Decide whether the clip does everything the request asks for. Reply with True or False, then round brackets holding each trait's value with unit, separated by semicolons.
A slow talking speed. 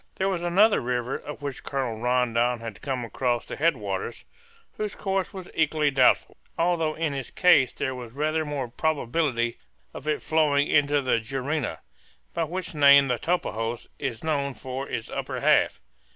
False (165 wpm)